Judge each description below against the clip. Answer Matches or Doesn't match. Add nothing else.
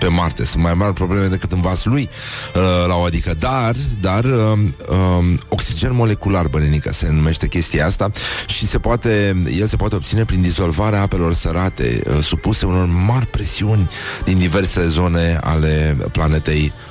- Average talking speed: Matches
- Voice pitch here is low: Matches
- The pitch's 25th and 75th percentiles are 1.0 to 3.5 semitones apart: Doesn't match